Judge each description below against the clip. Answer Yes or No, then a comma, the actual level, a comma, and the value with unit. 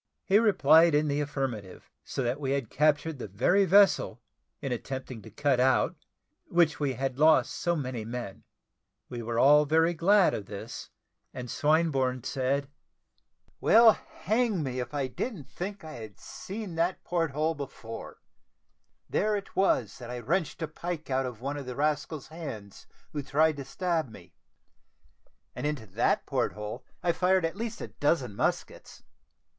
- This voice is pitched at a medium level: Yes, medium, 145 Hz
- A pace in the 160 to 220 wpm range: Yes, average, 165 wpm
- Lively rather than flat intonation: No, average, 4.9 semitones